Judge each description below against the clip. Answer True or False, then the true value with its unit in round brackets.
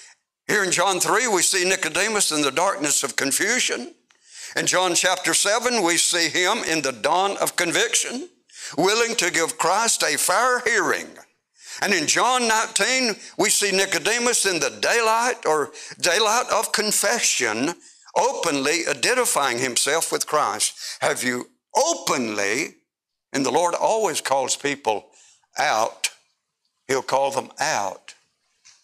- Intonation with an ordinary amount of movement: False (6.0 semitones)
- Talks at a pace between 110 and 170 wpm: True (135 wpm)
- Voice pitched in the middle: False (195 Hz)